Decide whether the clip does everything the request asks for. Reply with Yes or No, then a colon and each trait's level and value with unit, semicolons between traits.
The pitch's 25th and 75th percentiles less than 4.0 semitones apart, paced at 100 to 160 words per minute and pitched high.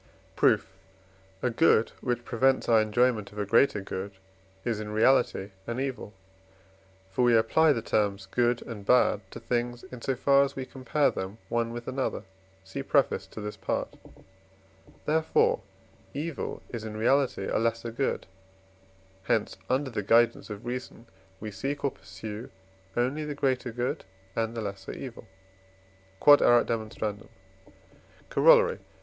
No: average, 3.6 semitones; average, 145 wpm; low, 120 Hz